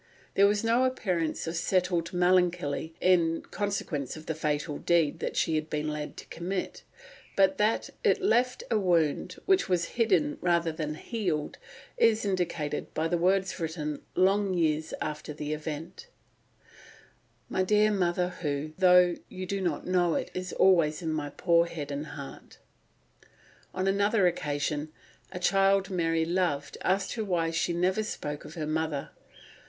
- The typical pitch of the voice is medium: Yes, medium, 175 Hz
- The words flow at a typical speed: Yes, average, 155 wpm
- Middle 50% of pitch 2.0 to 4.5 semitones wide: Yes, average, 3.6 semitones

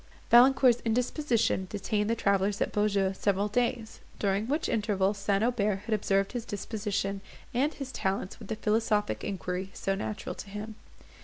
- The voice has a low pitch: No, high, 210 Hz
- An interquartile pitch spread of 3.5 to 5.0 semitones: No, average, 2.7 semitones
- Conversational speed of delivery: Yes, average, 155 wpm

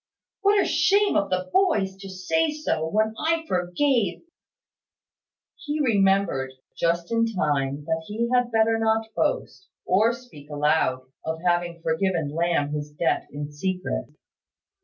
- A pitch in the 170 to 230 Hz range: Yes, high, 190 Hz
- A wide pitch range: Yes, wide, 6.2 semitones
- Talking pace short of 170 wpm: Yes, average, 140 wpm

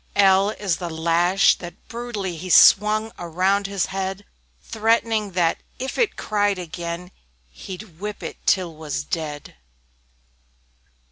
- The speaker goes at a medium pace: No, slow, 130 wpm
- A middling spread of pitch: Yes, average, 3.4 semitones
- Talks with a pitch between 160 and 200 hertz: Yes, high, 190 Hz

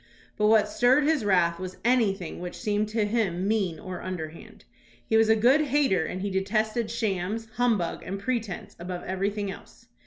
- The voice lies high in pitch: Yes, high, 205 Hz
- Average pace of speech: Yes, average, 175 wpm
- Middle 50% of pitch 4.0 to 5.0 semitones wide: No, average, 3.5 semitones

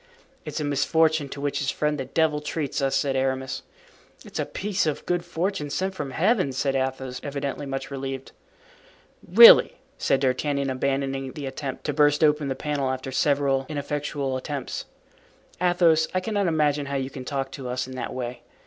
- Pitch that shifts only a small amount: Yes, narrow, 2.3 semitones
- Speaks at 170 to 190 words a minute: Yes, average, 175 wpm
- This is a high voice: No, medium, 140 Hz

